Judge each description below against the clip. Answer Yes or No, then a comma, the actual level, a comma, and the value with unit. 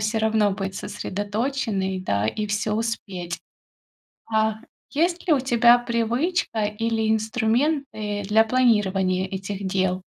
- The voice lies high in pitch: Yes, high, 215 Hz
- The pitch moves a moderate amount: Yes, average, 3.3 semitones